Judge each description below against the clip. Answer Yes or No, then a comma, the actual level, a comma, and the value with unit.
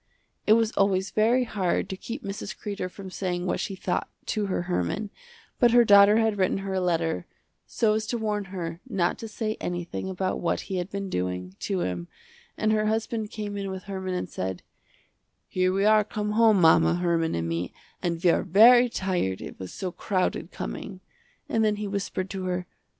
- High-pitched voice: Yes, high, 195 Hz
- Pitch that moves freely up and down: No, average, 3.1 semitones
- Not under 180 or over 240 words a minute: Yes, average, 200 wpm